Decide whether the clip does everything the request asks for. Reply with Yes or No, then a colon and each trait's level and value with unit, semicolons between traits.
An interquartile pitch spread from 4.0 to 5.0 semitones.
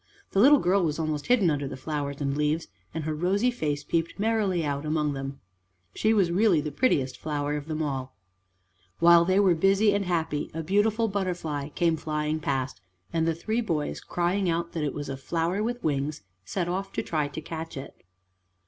Yes: average, 4.4 semitones